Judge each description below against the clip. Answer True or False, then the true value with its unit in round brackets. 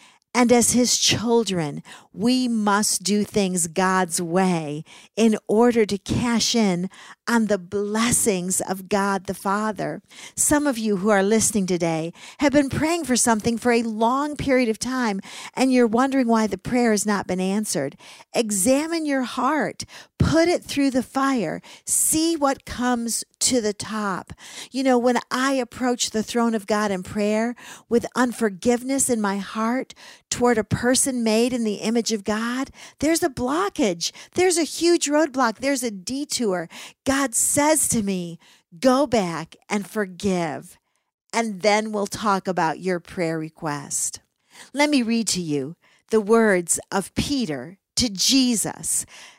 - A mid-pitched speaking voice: False (225 Hz)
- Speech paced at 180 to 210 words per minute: False (155 wpm)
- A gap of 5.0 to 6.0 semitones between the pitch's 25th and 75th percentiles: False (4.1 semitones)